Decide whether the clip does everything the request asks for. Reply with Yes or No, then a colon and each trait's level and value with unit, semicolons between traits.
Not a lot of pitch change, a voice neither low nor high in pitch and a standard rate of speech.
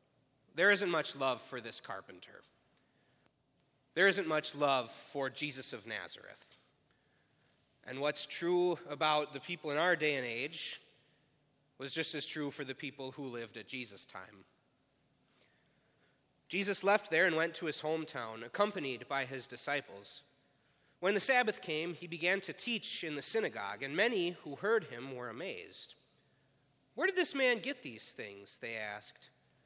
No: average, 5.0 semitones; medium, 150 Hz; average, 155 wpm